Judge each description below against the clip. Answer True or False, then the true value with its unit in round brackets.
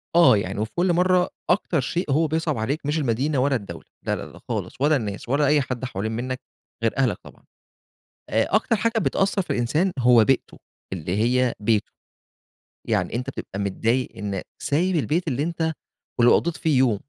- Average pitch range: False (6.1 semitones)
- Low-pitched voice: True (130 Hz)